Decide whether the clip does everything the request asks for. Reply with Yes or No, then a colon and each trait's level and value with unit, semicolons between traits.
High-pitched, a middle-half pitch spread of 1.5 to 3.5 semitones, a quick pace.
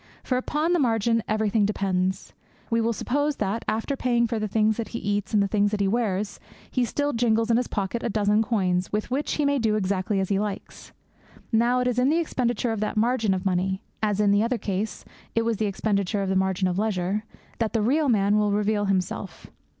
Yes: high, 215 Hz; average, 2.9 semitones; fast, 225 wpm